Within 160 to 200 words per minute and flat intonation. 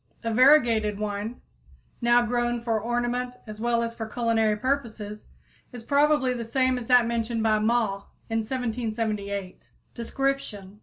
No: average, 140 wpm; narrow, 2.2 semitones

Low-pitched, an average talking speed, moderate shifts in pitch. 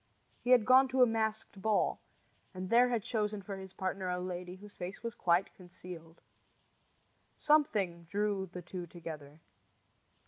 No: high, 190 Hz; average, 150 wpm; average, 3.6 semitones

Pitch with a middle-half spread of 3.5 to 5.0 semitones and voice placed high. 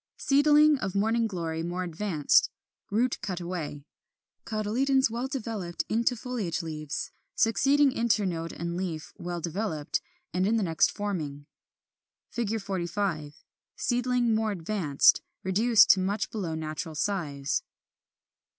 No: wide, 5.4 semitones; high, 195 Hz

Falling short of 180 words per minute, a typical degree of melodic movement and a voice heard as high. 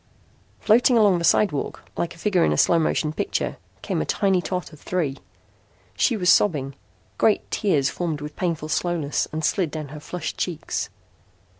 No: average, 170 wpm; average, 3.5 semitones; medium, 170 Hz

